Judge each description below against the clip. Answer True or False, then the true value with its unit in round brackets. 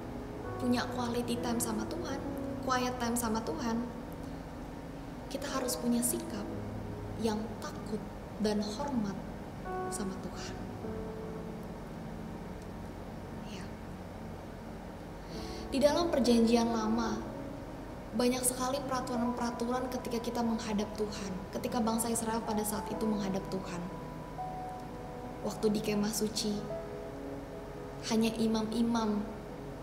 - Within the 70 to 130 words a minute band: True (90 wpm)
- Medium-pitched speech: False (225 Hz)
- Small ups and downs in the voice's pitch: True (2.1 semitones)